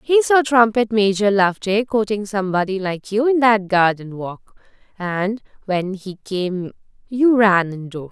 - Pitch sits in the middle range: No, high, 205 Hz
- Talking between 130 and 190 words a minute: Yes, average, 150 wpm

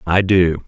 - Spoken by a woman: No, male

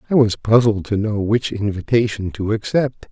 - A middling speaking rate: Yes, average, 175 wpm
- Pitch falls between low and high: No, low, 110 Hz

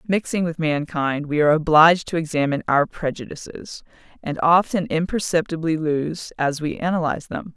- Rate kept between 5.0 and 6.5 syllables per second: Yes, 5.4 syllables/s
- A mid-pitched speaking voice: Yes, medium, 160 Hz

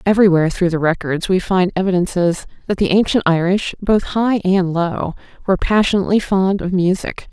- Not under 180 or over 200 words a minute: No, average, 165 wpm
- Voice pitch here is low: No, medium, 185 Hz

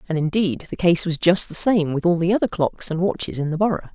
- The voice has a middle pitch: Yes, medium, 175 Hz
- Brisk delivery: Yes, fast, 275 wpm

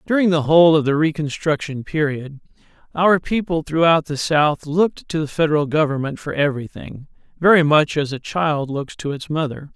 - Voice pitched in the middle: Yes, medium, 155 Hz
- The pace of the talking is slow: No, average, 170 wpm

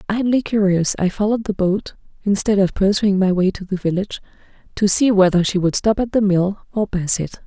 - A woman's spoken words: Yes, female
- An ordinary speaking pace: No, fast, 210 wpm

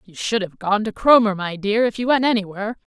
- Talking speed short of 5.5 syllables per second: No, 5.9 syllables/s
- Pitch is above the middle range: Yes, high, 210 Hz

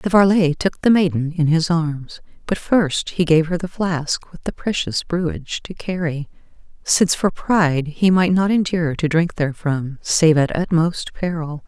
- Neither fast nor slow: Yes, average, 180 wpm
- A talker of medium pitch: Yes, medium, 170 Hz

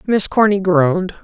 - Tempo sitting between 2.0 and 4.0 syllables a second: No, 4.8 syllables/s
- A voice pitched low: No, high, 200 Hz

